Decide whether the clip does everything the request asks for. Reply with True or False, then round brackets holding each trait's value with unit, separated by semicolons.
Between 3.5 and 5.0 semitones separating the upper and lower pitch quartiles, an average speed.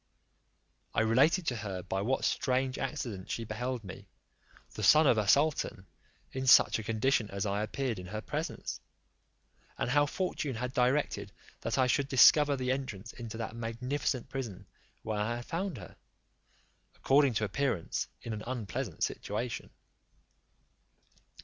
True (4.0 semitones; 150 wpm)